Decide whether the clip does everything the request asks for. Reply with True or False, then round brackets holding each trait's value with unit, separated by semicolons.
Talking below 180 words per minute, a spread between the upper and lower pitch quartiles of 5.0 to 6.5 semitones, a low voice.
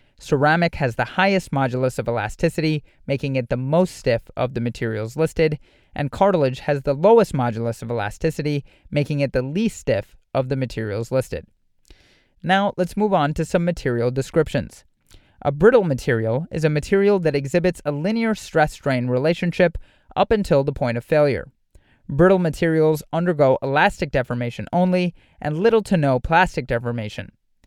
False (155 wpm; 5.6 semitones; 145 Hz)